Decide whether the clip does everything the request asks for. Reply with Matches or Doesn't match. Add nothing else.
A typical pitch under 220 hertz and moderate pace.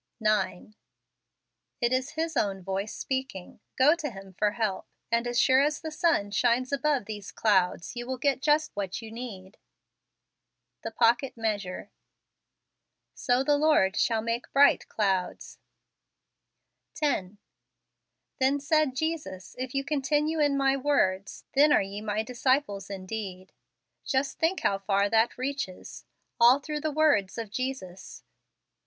Doesn't match